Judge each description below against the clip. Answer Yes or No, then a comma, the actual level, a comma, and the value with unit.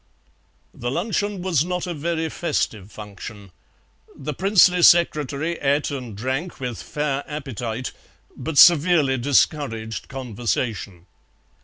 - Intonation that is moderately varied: No, wide, 6.0 semitones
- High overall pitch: No, medium, 140 Hz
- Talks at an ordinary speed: No, slow, 110 wpm